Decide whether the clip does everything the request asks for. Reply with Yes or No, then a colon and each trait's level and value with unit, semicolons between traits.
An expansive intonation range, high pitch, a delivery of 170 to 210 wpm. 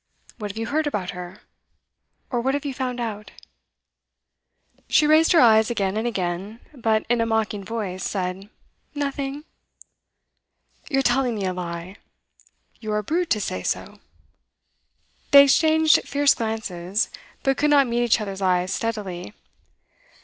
No: wide, 5.7 semitones; high, 225 Hz; average, 145 wpm